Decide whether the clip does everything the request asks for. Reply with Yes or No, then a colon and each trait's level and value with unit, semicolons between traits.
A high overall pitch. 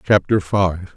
No: very low, 95 Hz